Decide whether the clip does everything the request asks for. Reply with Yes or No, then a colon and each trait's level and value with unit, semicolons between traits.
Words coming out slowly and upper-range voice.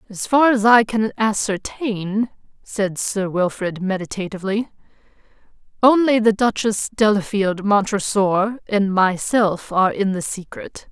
Yes: slow, 115 wpm; high, 205 Hz